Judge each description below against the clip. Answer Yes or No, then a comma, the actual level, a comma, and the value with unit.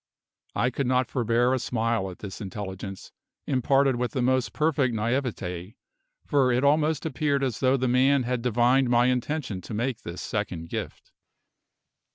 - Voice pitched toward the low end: Yes, low, 125 Hz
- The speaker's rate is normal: Yes, average, 160 wpm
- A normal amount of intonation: Yes, average, 3.2 semitones